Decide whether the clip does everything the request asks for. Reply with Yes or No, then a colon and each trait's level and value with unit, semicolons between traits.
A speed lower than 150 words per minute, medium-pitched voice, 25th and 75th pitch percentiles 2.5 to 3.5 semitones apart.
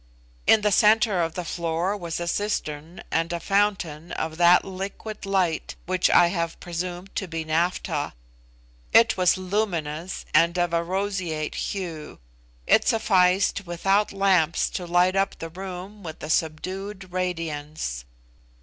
Yes: average, 140 wpm; medium, 180 Hz; average, 2.8 semitones